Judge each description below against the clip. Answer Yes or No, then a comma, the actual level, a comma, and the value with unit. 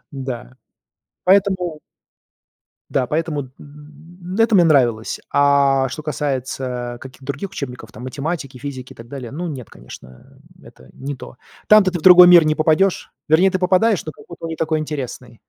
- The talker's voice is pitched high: No, medium, 150 Hz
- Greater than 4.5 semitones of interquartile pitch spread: Yes, average, 5.0 semitones